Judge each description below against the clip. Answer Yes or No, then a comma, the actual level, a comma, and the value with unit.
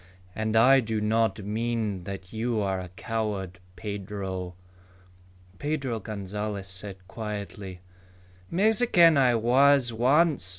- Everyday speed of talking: No, slow, 110 wpm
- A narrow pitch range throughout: No, average, 3.8 semitones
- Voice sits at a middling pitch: No, low, 110 Hz